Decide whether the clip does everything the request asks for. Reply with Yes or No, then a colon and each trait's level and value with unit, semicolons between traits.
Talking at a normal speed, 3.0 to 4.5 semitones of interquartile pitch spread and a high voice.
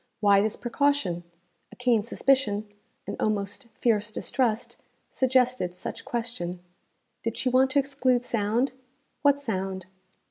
No: slow, 120 wpm; average, 4.1 semitones; high, 235 Hz